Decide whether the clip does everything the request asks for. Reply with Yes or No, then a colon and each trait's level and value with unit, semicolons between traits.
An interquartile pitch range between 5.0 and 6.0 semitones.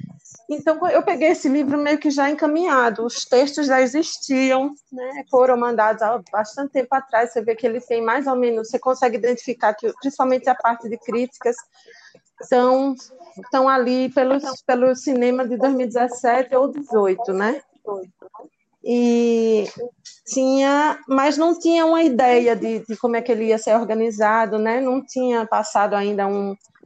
No: average, 3.1 semitones